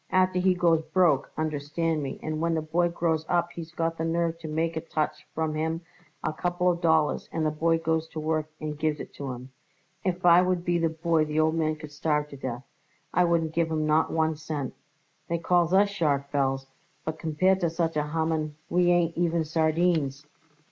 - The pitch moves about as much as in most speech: No, narrow, 1.8 semitones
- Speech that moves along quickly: Yes, fast, 210 wpm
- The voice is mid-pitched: Yes, medium, 160 Hz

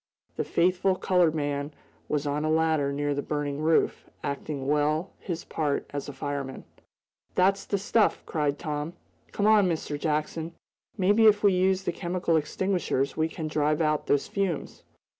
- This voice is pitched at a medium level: Yes, medium, 155 Hz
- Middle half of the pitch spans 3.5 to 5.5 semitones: Yes, average, 3.9 semitones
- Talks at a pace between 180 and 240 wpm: No, average, 160 wpm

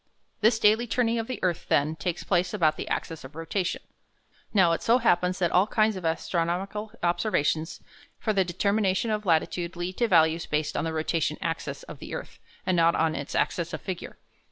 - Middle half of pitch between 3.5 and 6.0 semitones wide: Yes, average, 4.3 semitones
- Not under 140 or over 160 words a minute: No, average, 195 wpm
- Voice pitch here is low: No, medium, 180 Hz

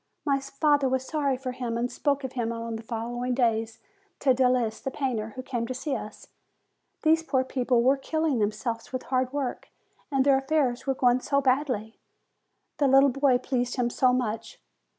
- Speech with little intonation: Yes, narrow, 2.3 semitones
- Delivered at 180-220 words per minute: Yes, average, 185 wpm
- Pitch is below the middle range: No, very high, 255 Hz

